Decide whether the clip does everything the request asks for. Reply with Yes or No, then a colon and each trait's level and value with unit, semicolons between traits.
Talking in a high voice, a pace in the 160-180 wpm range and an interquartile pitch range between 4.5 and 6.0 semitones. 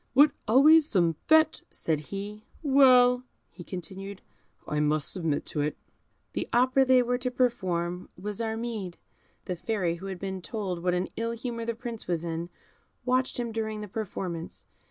Yes: high, 210 Hz; average, 165 wpm; wide, 5.6 semitones